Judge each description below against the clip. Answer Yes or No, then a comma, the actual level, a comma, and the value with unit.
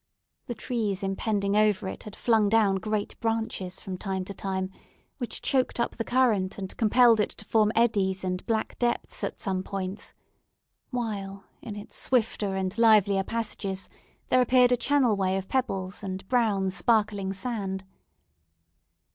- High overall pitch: Yes, high, 205 Hz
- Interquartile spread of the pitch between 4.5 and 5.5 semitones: No, average, 3.1 semitones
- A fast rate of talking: No, average, 155 wpm